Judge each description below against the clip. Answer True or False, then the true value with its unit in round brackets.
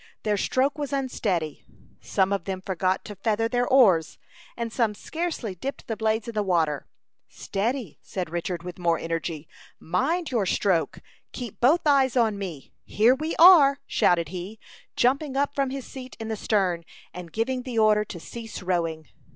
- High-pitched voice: True (215 Hz)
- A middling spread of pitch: False (6.3 semitones)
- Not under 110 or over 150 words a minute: False (170 wpm)